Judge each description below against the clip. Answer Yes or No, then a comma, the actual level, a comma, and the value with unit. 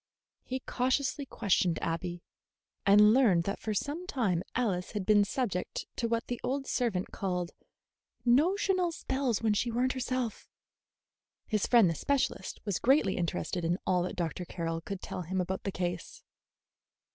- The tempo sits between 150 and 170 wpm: Yes, average, 160 wpm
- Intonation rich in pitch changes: Yes, wide, 6.0 semitones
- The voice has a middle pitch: No, high, 210 Hz